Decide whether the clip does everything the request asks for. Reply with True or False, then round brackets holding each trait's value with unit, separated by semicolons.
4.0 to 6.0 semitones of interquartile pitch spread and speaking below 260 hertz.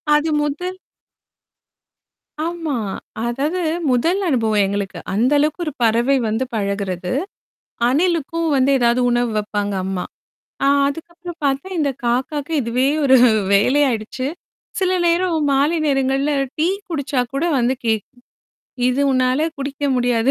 False (4.5 semitones; 270 Hz)